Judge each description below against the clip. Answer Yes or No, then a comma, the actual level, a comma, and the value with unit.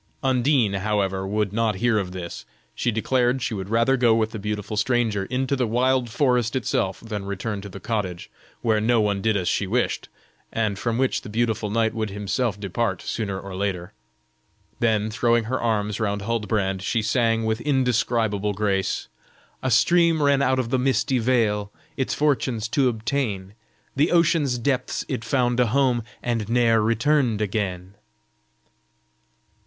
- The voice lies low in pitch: Yes, low, 115 Hz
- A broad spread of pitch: No, average, 3.2 semitones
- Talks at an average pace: Yes, average, 160 wpm